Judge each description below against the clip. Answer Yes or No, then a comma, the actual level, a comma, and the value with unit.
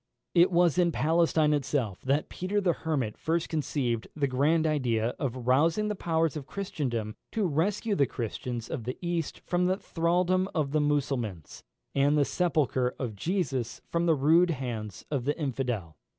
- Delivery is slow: No, average, 165 wpm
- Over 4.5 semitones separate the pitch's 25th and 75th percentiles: Yes, average, 5.1 semitones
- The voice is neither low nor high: Yes, medium, 150 Hz